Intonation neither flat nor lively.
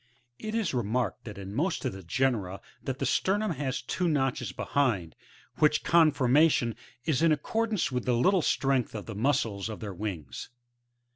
No: wide, 6.5 semitones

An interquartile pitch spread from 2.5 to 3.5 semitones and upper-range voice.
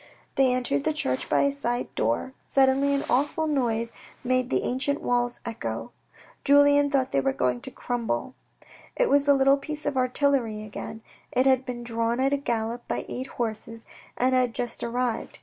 Yes: average, 3.2 semitones; very high, 255 Hz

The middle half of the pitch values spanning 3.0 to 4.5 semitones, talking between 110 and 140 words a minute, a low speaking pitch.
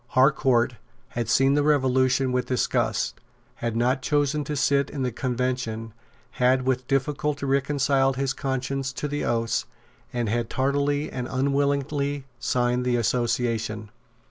No: narrow, 2.4 semitones; slow, 135 wpm; low, 130 Hz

